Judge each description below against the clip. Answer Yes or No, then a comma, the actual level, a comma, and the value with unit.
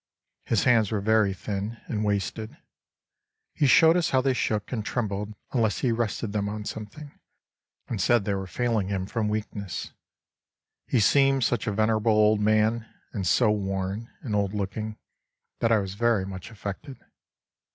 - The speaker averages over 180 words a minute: No, average, 160 wpm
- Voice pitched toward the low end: Yes, low, 110 Hz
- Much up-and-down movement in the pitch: No, narrow, 2.6 semitones